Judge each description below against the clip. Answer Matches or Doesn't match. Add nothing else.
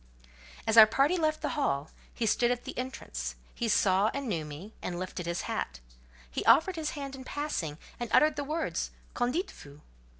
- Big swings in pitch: Matches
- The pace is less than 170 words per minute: Doesn't match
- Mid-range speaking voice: Doesn't match